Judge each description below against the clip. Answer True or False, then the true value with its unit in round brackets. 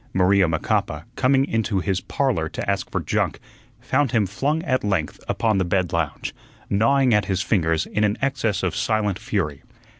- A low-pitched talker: True (105 Hz)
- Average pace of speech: True (175 wpm)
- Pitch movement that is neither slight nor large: True (4.3 semitones)